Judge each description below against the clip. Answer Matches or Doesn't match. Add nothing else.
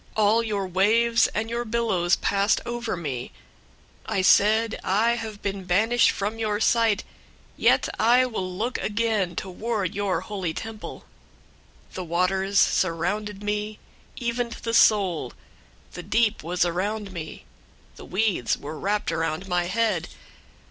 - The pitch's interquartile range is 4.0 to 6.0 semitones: Doesn't match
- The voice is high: Matches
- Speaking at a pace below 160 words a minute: Matches